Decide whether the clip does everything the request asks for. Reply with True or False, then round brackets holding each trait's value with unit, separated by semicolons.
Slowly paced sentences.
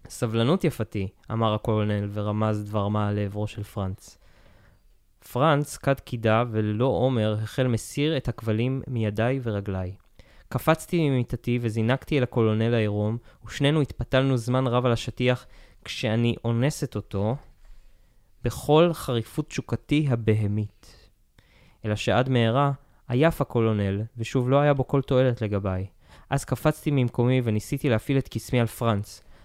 False (125 wpm)